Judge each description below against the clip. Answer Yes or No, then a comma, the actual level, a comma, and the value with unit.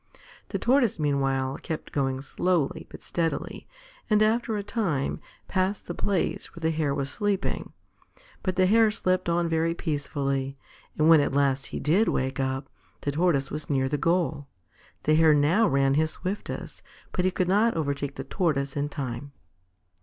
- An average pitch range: Yes, average, 4.9 semitones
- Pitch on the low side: No, medium, 155 Hz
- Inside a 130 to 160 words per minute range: No, average, 170 wpm